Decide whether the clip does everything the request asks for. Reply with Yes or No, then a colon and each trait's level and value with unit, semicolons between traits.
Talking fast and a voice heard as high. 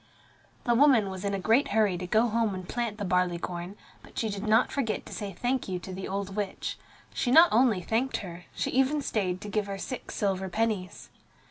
Yes: fast, 220 wpm; high, 205 Hz